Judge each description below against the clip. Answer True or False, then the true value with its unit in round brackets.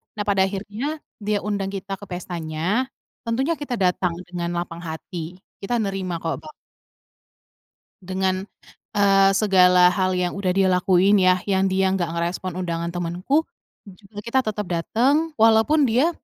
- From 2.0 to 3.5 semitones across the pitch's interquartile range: True (2.8 semitones)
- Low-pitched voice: False (190 Hz)